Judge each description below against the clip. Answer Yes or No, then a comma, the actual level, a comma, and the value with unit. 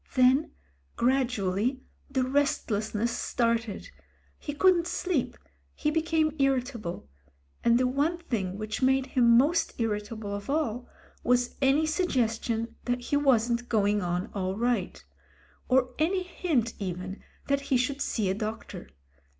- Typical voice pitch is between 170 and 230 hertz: No, high, 245 Hz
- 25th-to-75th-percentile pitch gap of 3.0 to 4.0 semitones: No, average, 4.5 semitones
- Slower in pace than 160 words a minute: Yes, slow, 135 wpm